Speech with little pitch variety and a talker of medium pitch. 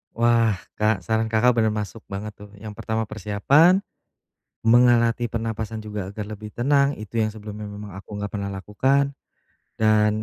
No: narrow, 2.0 semitones; low, 110 Hz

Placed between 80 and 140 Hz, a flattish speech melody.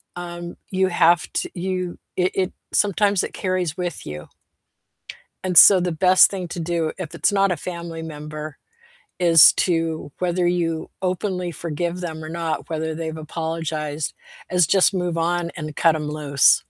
No: medium, 170 Hz; narrow, 2.2 semitones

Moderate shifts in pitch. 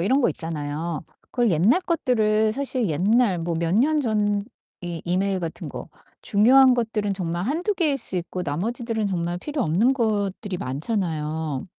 No: wide, 6.0 semitones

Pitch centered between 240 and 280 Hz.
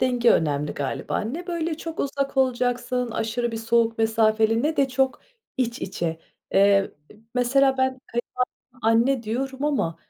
Yes: high, 245 Hz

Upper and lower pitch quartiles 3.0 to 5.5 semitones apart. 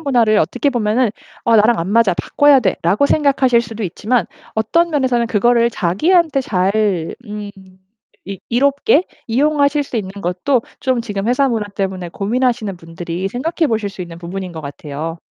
Yes: average, 5.2 semitones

